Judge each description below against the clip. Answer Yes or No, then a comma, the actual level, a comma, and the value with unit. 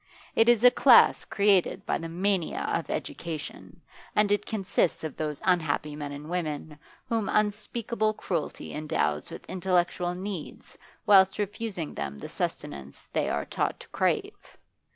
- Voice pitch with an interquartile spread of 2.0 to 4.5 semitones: No, average, 5.1 semitones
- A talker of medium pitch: Yes, medium, 180 Hz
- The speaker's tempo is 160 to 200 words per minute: No, average, 145 wpm